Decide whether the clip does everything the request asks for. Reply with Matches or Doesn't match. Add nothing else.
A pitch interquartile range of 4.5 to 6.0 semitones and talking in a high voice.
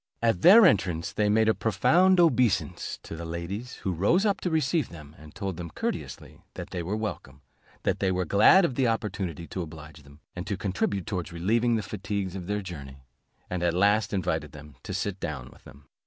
Doesn't match